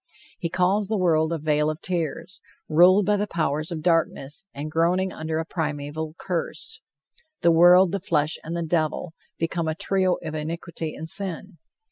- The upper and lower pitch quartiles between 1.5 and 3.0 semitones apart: Yes, narrow, 2.6 semitones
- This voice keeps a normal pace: Yes, average, 170 wpm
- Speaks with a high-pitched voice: No, medium, 165 Hz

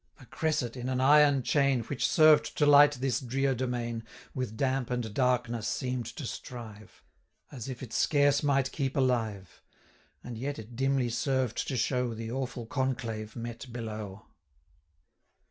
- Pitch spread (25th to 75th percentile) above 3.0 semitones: No, narrow, 2.6 semitones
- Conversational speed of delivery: Yes, average, 155 wpm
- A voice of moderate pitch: No, low, 125 Hz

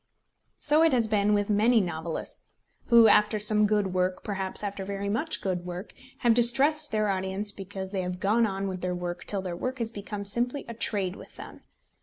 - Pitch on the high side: Yes, high, 205 Hz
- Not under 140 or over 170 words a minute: No, average, 200 wpm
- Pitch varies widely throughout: No, average, 3.0 semitones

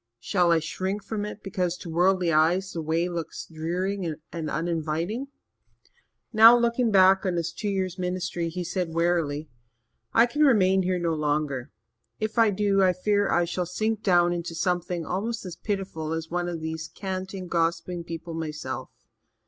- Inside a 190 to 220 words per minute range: No, average, 165 wpm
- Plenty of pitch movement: No, average, 2.8 semitones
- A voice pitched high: No, medium, 180 Hz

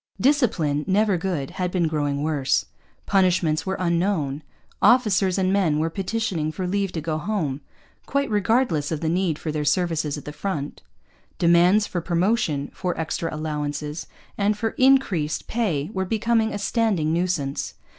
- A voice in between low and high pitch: Yes, medium, 175 Hz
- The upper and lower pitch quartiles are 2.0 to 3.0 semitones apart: No, average, 4.7 semitones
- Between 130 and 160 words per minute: Yes, average, 155 wpm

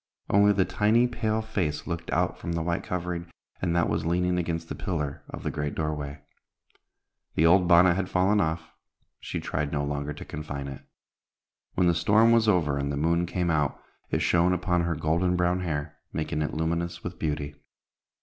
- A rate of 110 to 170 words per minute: No, average, 190 wpm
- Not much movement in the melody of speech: No, average, 3.0 semitones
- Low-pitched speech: Yes, very low, 85 Hz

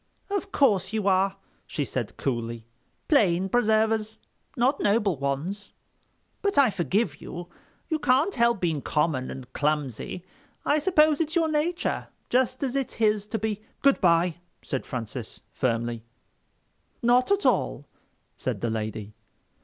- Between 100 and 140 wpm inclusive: Yes, slow, 135 wpm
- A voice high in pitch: Yes, high, 200 Hz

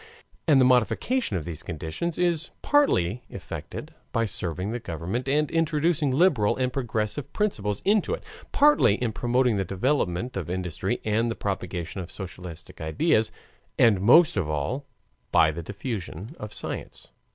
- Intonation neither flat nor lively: No, wide, 8.0 semitones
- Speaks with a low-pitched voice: Yes, low, 110 Hz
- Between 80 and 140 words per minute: No, average, 150 wpm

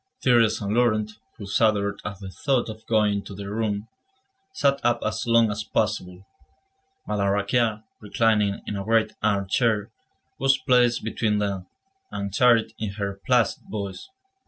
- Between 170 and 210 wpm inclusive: No, average, 150 wpm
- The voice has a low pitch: Yes, low, 105 Hz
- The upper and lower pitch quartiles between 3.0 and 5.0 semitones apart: No, narrow, 2.5 semitones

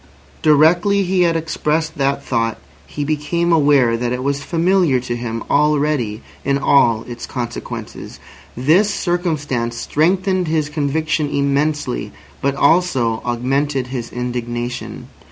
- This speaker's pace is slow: Yes, slow, 120 wpm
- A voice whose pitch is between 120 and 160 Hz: Yes, medium, 140 Hz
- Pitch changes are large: No, average, 4.6 semitones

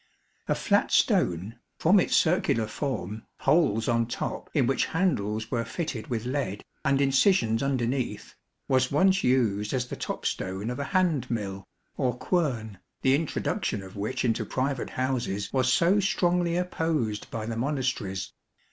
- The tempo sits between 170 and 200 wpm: No, average, 155 wpm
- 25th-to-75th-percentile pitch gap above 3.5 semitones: Yes, average, 5.0 semitones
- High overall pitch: No, low, 125 Hz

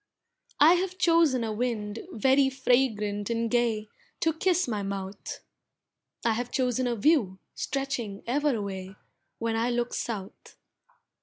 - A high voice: Yes, high, 240 Hz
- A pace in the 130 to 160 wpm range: Yes, slow, 135 wpm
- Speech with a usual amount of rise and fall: Yes, average, 4.3 semitones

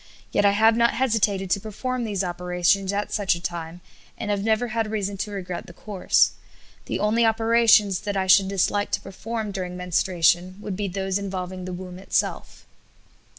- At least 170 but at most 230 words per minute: Yes, average, 180 wpm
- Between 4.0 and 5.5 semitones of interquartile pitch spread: No, average, 2.7 semitones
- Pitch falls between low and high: No, high, 195 Hz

